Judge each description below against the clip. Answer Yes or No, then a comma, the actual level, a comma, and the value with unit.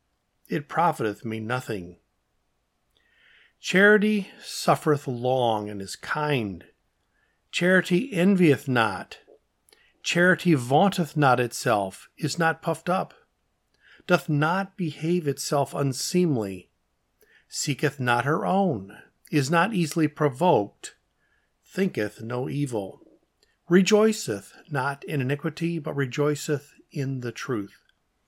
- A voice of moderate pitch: Yes, medium, 150 Hz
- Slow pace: Yes, slow, 100 wpm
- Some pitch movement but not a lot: No, wide, 5.8 semitones